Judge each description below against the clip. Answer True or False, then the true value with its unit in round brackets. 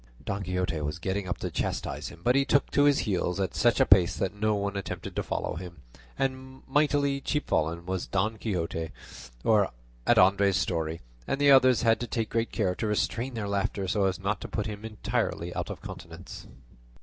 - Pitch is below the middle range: True (100 Hz)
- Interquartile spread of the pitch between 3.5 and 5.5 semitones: True (4.4 semitones)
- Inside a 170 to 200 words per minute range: True (195 wpm)